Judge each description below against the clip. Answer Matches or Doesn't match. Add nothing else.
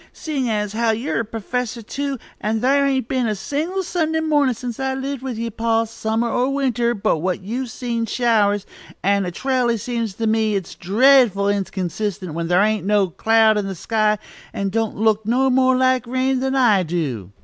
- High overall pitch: Matches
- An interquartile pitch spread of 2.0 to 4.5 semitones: Matches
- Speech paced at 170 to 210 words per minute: Matches